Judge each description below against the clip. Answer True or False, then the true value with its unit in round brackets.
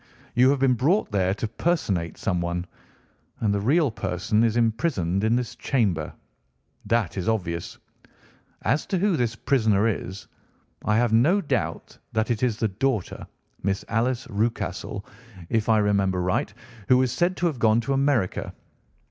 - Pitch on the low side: True (110 Hz)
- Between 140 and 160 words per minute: True (155 wpm)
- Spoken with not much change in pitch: False (4.5 semitones)